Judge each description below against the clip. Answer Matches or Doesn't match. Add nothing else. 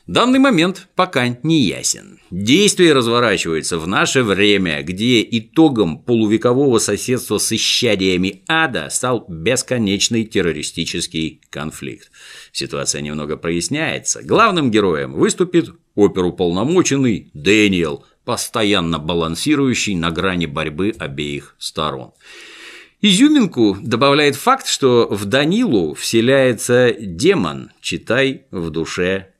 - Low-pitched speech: Matches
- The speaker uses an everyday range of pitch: Doesn't match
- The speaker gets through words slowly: Matches